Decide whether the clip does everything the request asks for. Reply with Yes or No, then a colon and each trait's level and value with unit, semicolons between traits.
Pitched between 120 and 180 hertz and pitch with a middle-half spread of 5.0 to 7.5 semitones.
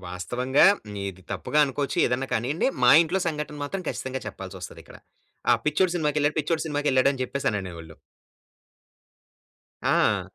Yes: low, 135 Hz; wide, 5.4 semitones